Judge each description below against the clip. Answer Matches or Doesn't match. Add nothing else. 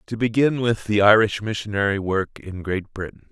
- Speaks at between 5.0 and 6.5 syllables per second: Matches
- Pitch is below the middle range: Matches